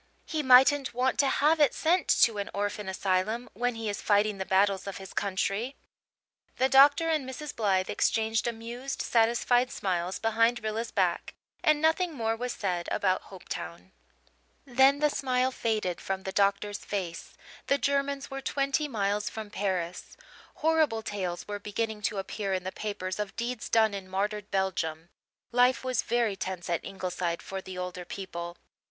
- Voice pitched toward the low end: No, high, 215 Hz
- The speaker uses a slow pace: No, average, 165 wpm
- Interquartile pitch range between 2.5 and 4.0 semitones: No, average, 4.9 semitones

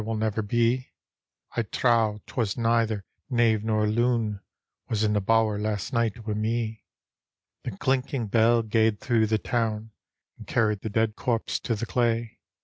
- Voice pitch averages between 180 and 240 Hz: No, low, 110 Hz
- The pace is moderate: Yes, average, 155 wpm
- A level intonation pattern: Yes, narrow, 1.6 semitones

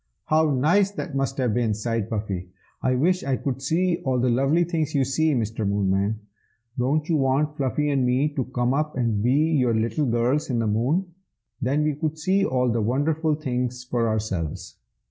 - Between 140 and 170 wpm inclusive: No, average, 190 wpm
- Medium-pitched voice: No, low, 130 Hz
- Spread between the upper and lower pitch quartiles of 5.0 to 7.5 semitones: No, average, 4.6 semitones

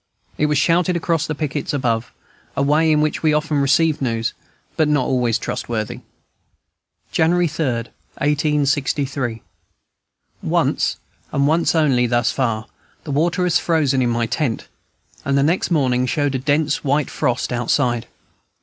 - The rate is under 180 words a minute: Yes, average, 150 wpm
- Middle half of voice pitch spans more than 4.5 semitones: No, average, 3.9 semitones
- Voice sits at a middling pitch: Yes, medium, 145 Hz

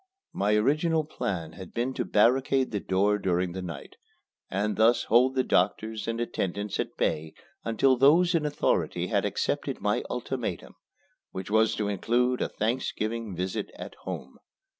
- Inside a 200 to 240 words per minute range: No, average, 155 wpm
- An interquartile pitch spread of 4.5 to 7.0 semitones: Yes, average, 5.0 semitones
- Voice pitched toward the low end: Yes, low, 110 Hz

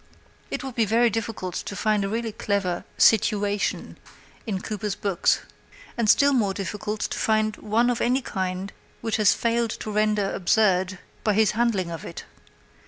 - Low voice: No, high, 210 Hz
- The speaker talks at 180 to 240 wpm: No, average, 170 wpm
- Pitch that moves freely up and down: No, narrow, 2.5 semitones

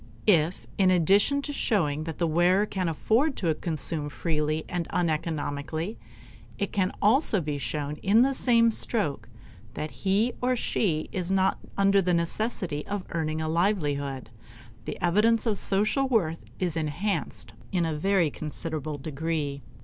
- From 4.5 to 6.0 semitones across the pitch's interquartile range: Yes, average, 4.8 semitones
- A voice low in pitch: No, medium, 175 Hz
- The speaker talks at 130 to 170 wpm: Yes, average, 150 wpm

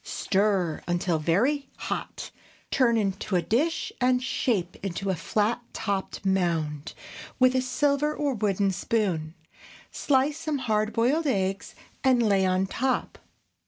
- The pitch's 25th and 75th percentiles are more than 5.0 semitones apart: Yes, wide, 5.5 semitones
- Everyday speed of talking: No, slow, 130 wpm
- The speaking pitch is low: No, high, 215 Hz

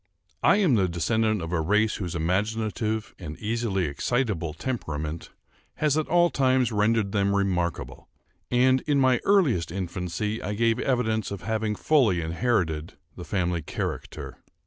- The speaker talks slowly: No, average, 145 wpm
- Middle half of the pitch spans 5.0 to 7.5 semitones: Yes, wide, 5.5 semitones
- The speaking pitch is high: No, low, 105 Hz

